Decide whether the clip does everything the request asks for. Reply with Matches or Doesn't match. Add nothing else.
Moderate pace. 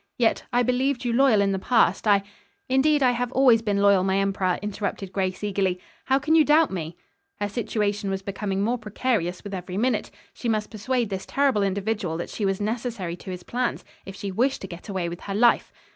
Doesn't match